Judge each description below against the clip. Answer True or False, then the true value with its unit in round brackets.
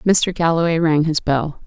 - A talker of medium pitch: True (160 Hz)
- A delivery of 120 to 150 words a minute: False (180 wpm)